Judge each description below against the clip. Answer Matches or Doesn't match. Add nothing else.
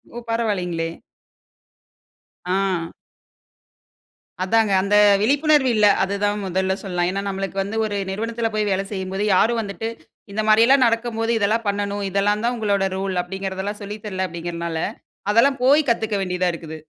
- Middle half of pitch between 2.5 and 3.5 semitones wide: Matches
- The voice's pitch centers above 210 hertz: Doesn't match